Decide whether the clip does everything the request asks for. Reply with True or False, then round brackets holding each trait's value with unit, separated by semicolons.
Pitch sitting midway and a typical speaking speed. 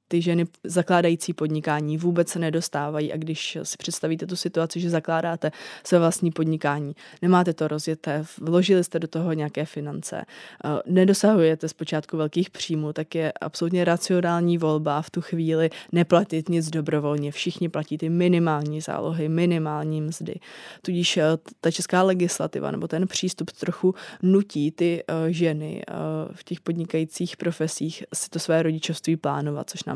True (165 Hz; 140 wpm)